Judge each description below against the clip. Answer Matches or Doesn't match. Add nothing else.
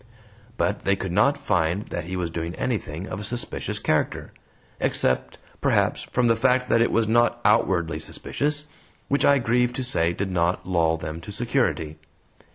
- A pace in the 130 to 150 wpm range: Doesn't match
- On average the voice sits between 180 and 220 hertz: Doesn't match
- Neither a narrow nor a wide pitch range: Doesn't match